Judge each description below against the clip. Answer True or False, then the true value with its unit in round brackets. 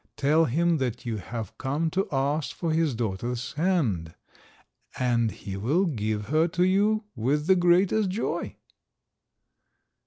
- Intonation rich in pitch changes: True (6.7 semitones)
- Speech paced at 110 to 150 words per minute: True (135 wpm)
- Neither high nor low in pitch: True (145 Hz)